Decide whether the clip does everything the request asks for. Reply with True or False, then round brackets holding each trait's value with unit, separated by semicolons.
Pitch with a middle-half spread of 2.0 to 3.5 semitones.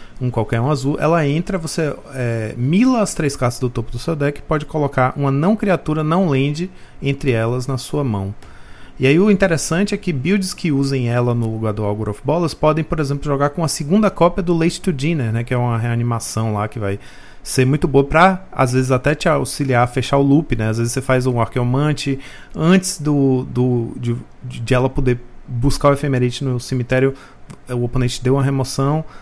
False (4.2 semitones)